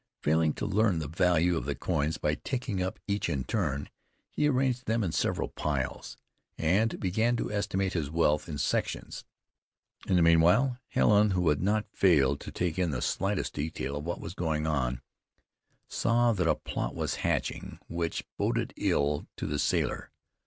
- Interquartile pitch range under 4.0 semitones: No, wide, 5.4 semitones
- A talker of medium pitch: No, very low, 85 Hz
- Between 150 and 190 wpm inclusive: Yes, average, 175 wpm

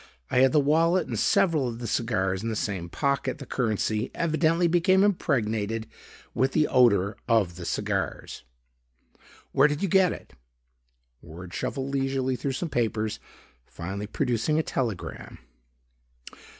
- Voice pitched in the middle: No, low, 125 Hz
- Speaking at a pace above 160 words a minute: No, average, 140 wpm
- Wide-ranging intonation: Yes, wide, 6.0 semitones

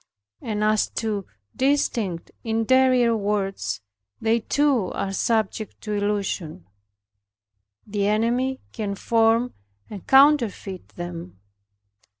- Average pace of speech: No, slow, 95 wpm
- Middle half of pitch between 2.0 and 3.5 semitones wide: Yes, average, 3.0 semitones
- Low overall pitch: No, high, 215 Hz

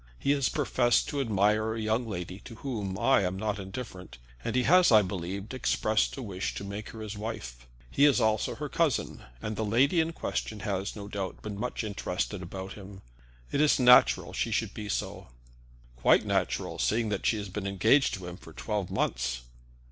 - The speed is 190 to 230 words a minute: Yes, average, 195 wpm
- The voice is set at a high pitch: No, low, 105 Hz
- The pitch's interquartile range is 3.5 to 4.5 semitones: Yes, average, 3.9 semitones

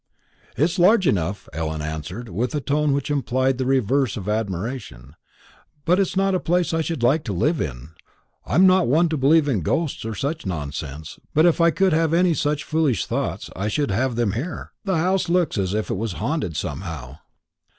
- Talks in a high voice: No, low, 130 Hz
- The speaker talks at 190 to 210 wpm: Yes, average, 195 wpm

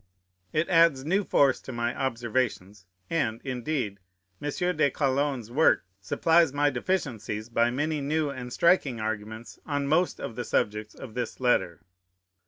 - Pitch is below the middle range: Yes, low, 130 Hz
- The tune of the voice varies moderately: Yes, average, 4.4 semitones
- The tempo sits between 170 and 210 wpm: No, average, 145 wpm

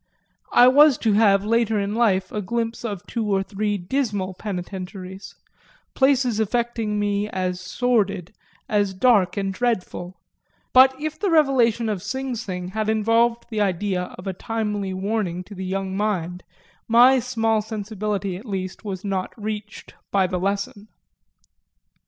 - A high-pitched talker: Yes, high, 210 Hz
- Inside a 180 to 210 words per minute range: No, average, 145 wpm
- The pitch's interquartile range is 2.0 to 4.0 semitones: Yes, average, 3.3 semitones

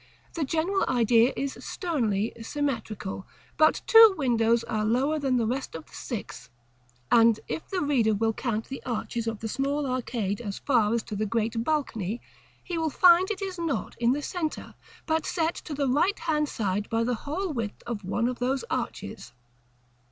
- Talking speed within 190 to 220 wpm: No, average, 180 wpm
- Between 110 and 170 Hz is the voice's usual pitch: No, very high, 250 Hz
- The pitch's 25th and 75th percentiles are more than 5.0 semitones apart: Yes, wide, 5.4 semitones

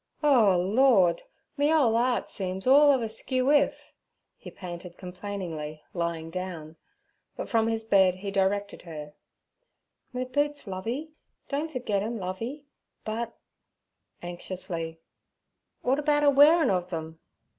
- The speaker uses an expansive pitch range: Yes, wide, 6.4 semitones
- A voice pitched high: Yes, high, 205 Hz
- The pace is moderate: No, slow, 115 wpm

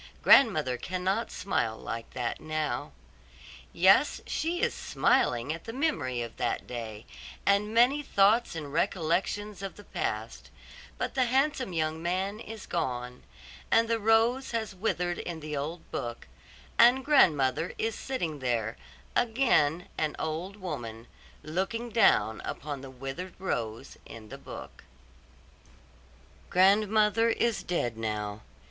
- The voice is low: No, medium, 180 Hz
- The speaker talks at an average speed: No, slow, 130 wpm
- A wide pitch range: Yes, wide, 8.8 semitones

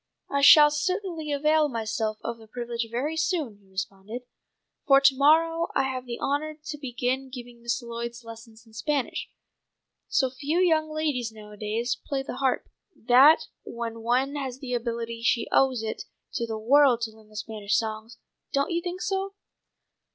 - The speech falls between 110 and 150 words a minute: No, average, 165 wpm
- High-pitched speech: Yes, very high, 250 Hz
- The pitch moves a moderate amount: Yes, average, 4.4 semitones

